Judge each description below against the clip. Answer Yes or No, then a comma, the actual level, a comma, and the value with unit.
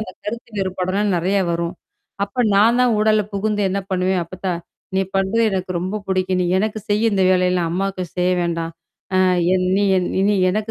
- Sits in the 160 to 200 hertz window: Yes, high, 190 Hz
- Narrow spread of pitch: Yes, narrow, 2.3 semitones